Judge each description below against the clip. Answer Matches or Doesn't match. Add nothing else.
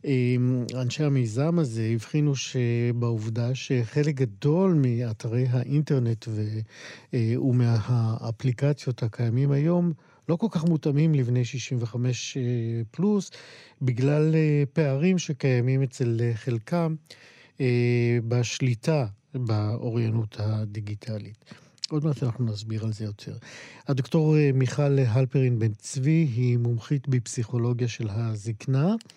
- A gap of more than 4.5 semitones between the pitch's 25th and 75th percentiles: Doesn't match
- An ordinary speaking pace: Doesn't match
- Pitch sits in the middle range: Doesn't match